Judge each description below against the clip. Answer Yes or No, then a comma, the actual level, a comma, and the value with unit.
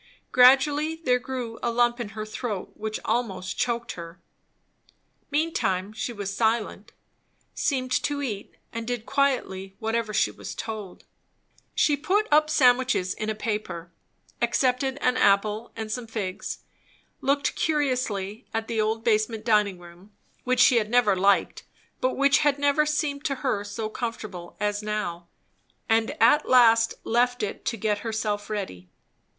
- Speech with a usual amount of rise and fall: Yes, average, 3.6 semitones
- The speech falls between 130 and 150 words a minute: Yes, average, 145 wpm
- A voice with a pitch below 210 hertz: No, high, 225 Hz